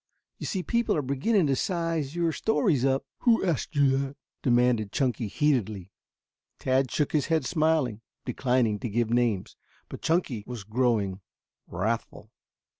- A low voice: Yes, low, 130 Hz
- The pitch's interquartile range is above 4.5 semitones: Yes, wide, 5.4 semitones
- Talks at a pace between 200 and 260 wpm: No, average, 145 wpm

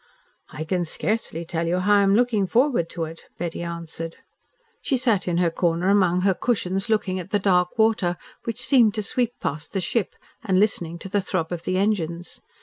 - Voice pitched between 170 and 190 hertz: Yes, medium, 185 Hz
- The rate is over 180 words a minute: Yes, average, 200 wpm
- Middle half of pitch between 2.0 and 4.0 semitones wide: Yes, average, 3.7 semitones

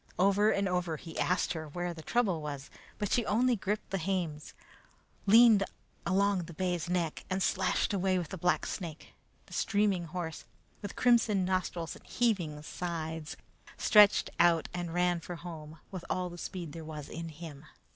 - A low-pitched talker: No, medium, 180 Hz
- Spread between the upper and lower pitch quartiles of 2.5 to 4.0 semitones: Yes, average, 3.1 semitones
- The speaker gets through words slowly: No, average, 165 wpm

